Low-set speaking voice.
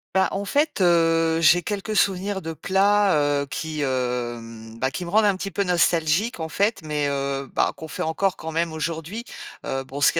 No: medium, 165 Hz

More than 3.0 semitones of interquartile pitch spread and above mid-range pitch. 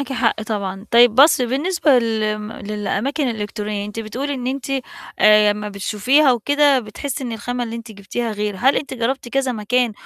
Yes: average, 3.8 semitones; high, 230 Hz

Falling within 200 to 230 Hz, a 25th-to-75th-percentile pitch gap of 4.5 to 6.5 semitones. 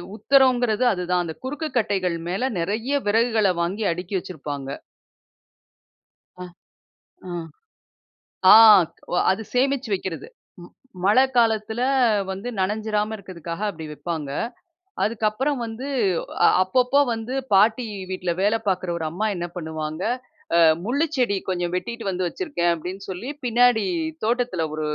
Yes: high, 205 Hz; average, 5.0 semitones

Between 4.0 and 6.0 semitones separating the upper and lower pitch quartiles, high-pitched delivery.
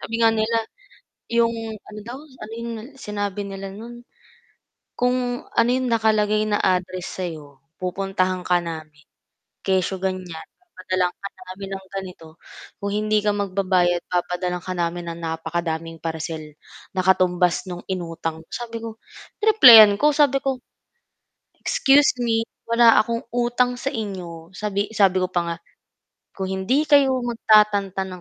Yes: average, 4.3 semitones; high, 195 Hz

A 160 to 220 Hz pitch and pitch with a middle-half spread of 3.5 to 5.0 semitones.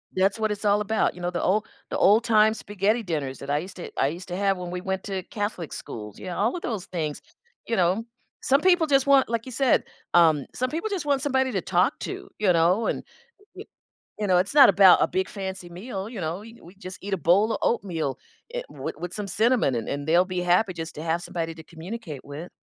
Yes: high, 190 Hz; average, 4.4 semitones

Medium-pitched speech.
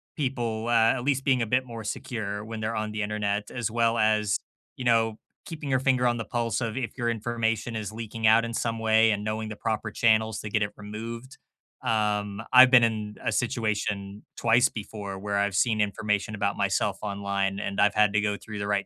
No: low, 110 Hz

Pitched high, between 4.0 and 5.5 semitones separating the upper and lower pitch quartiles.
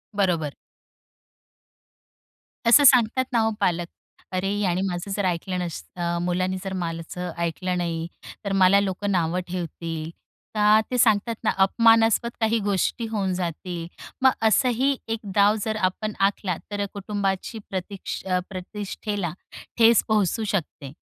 No: high, 195 Hz; average, 3.6 semitones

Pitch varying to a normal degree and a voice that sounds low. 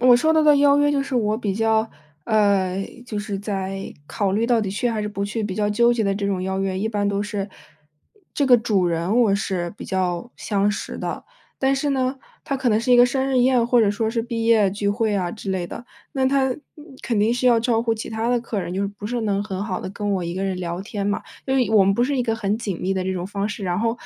No: average, 3.5 semitones; high, 215 Hz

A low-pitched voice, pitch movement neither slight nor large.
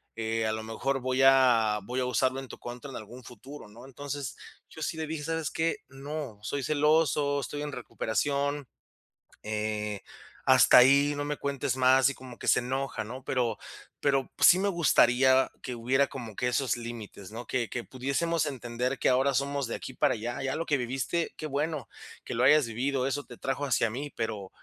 Yes: low, 130 Hz; average, 3.1 semitones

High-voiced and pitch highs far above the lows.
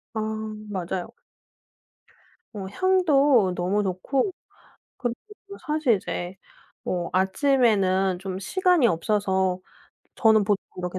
Yes: high, 200 Hz; wide, 6.3 semitones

